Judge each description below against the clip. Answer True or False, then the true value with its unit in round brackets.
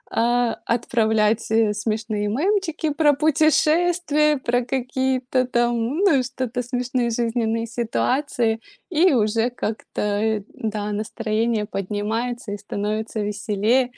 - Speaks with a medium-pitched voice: False (235 Hz)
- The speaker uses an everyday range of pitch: True (3.3 semitones)